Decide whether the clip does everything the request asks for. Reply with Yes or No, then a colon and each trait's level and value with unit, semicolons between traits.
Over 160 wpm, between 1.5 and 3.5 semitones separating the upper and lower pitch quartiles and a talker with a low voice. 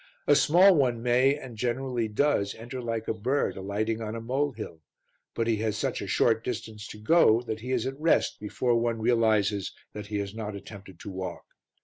Yes: average, 200 wpm; average, 3.0 semitones; low, 115 Hz